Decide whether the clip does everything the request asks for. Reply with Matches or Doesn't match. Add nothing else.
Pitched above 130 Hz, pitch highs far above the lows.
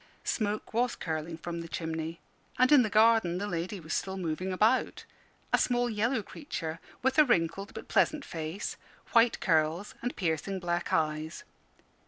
Matches